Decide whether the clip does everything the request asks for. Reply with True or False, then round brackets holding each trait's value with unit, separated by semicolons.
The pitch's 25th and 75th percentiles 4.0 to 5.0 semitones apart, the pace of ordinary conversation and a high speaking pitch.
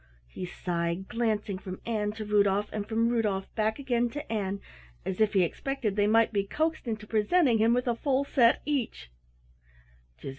False (3.1 semitones; 175 wpm; 220 Hz)